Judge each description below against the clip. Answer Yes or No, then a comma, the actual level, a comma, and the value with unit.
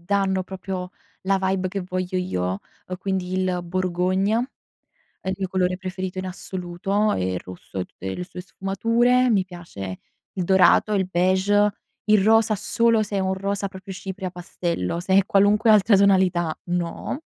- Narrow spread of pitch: Yes, narrow, 1.8 semitones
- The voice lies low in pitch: No, high, 190 Hz